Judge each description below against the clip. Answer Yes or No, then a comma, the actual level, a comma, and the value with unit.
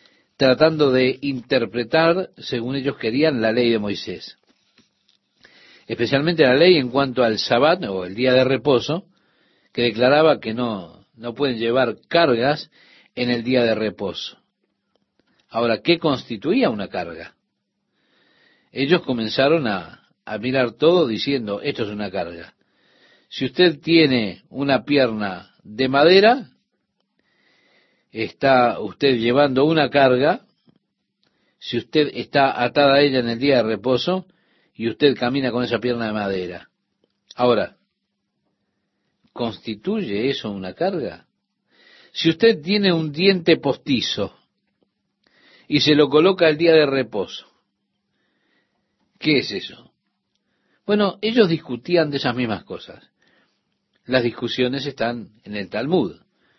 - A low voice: Yes, low, 130 Hz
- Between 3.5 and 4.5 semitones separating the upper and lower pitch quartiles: No, average, 5.0 semitones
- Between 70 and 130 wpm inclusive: Yes, slow, 125 wpm